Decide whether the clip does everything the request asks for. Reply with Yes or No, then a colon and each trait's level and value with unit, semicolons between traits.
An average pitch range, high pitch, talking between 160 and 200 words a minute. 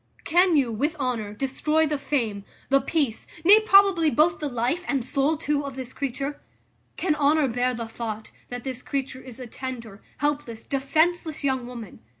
Yes: average, 3.8 semitones; very high, 275 Hz; average, 170 wpm